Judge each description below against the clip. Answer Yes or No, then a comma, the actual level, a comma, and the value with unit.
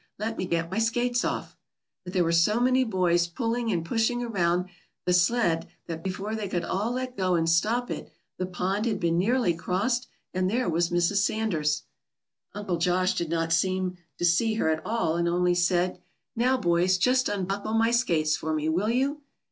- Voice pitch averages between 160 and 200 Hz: Yes, medium, 185 Hz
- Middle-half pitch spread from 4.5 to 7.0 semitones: Yes, average, 4.8 semitones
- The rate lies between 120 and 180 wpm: No, average, 190 wpm